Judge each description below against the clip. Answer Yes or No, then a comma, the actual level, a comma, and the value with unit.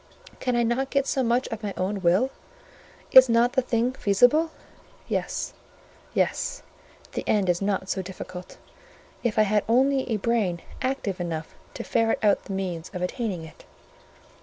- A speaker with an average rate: Yes, average, 155 wpm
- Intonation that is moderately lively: Yes, average, 5.0 semitones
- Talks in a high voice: Yes, high, 215 Hz